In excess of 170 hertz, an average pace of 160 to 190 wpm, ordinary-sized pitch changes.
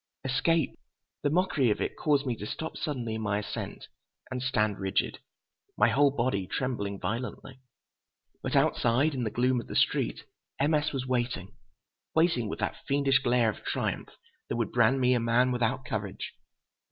No: low, 125 Hz; average, 170 wpm; average, 3.4 semitones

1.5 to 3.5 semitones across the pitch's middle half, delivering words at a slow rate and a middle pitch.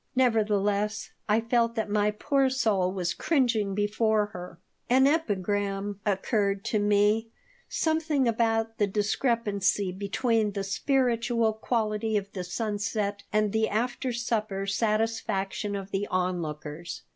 No: narrow, 2.5 semitones; slow, 120 wpm; high, 210 Hz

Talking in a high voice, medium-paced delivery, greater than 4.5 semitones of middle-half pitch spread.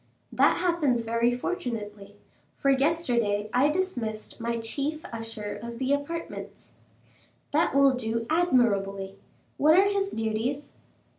No: high, 245 Hz; slow, 120 wpm; average, 5.1 semitones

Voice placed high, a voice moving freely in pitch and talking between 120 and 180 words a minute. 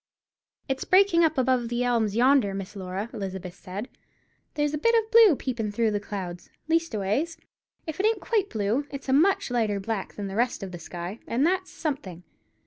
No: high, 240 Hz; wide, 7.5 semitones; average, 190 wpm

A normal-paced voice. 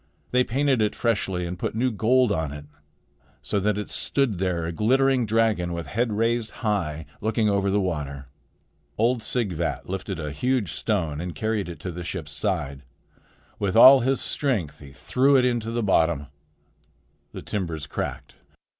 Yes: average, 165 wpm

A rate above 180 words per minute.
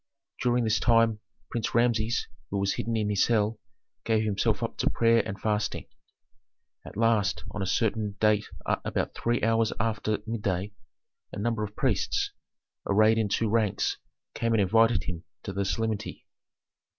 No: average, 155 wpm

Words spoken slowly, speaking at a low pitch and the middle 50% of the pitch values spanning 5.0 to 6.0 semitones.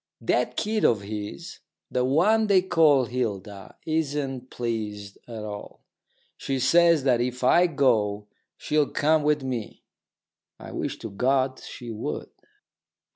Yes: slow, 130 wpm; low, 130 Hz; wide, 5.6 semitones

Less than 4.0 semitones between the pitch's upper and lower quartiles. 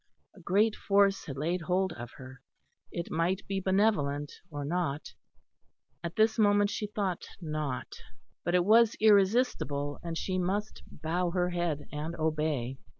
No: average, 4.7 semitones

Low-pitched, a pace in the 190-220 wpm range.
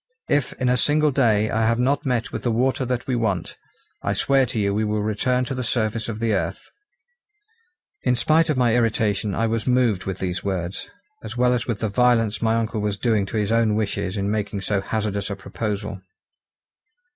Yes: low, 110 Hz; fast, 205 wpm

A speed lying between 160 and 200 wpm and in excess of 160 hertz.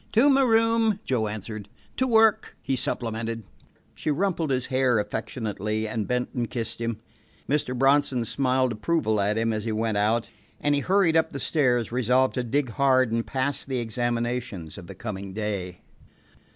No: average, 170 wpm; low, 120 Hz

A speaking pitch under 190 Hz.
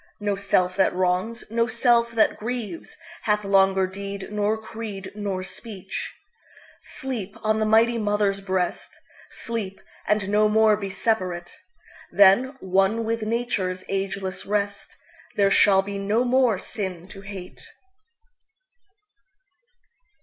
No: high, 205 Hz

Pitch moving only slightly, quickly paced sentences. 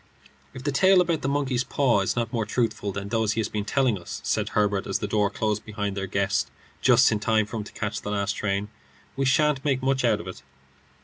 No: average, 4.4 semitones; fast, 240 wpm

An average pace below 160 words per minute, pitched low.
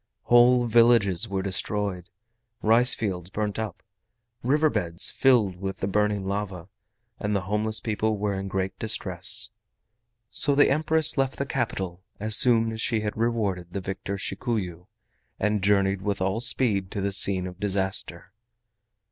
Yes: average, 150 wpm; low, 105 Hz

